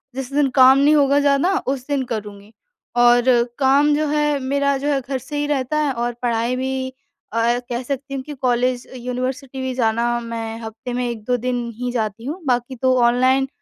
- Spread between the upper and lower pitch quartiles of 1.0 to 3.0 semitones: Yes, narrow, 2.4 semitones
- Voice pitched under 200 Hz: No, very high, 255 Hz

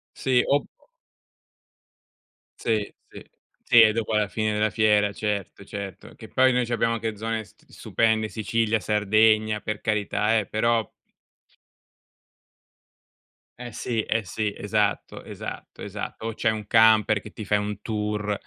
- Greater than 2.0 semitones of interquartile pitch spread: No, narrow, 1.3 semitones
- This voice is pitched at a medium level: No, low, 110 Hz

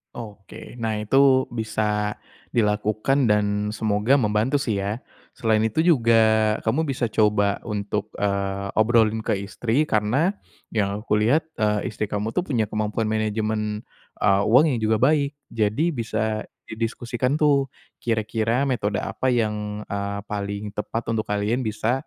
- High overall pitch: No, low, 110 Hz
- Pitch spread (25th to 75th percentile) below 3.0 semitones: Yes, narrow, 2.4 semitones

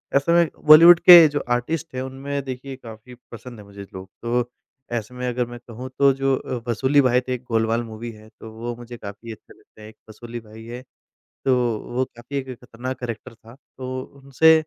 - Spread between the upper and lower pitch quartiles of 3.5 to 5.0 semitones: No, average, 2.7 semitones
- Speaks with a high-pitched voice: No, low, 125 Hz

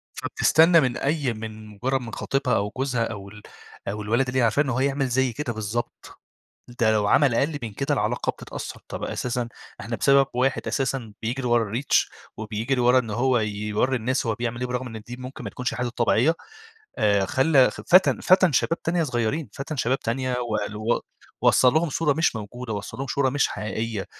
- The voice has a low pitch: Yes, low, 125 Hz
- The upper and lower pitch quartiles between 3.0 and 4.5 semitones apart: Yes, average, 3.4 semitones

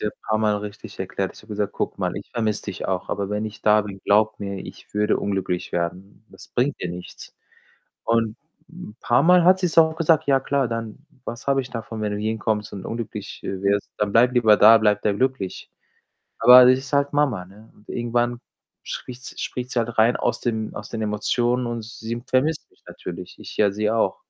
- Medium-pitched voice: No, low, 110 Hz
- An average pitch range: Yes, average, 3.0 semitones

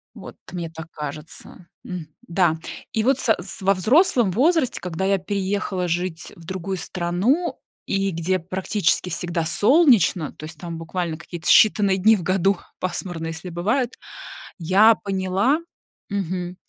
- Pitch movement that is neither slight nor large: Yes, average, 3.0 semitones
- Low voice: No, medium, 185 Hz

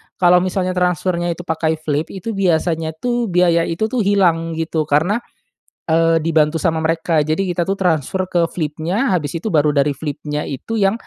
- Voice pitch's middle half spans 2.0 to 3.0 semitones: Yes, narrow, 2.6 semitones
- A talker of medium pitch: Yes, medium, 165 Hz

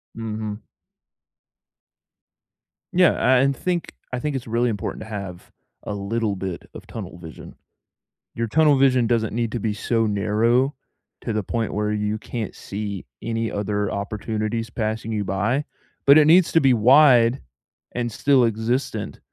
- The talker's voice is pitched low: Yes, low, 115 Hz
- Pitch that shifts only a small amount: No, average, 3.1 semitones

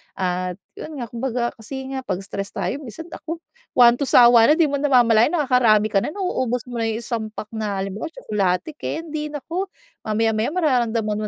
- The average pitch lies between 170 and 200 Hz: No, high, 235 Hz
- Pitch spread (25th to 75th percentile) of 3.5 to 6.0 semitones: Yes, average, 4.9 semitones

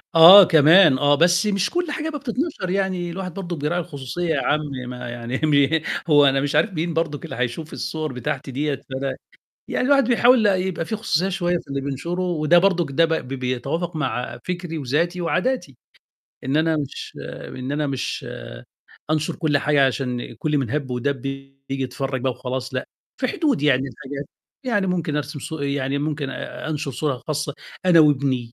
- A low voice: No, medium, 150 Hz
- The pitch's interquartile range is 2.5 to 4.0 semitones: No, average, 4.4 semitones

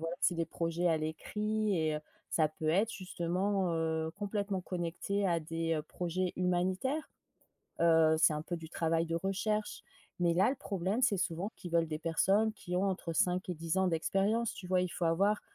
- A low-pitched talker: No, medium, 180 Hz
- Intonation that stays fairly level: No, average, 3.2 semitones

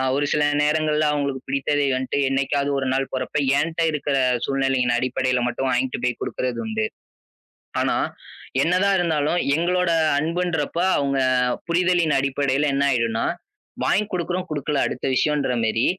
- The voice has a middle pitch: Yes, medium, 145 Hz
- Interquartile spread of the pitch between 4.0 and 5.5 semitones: No, average, 3.6 semitones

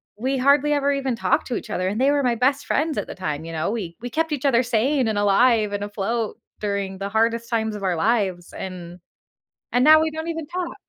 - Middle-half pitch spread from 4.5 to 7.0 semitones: Yes, wide, 5.6 semitones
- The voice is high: Yes, high, 230 Hz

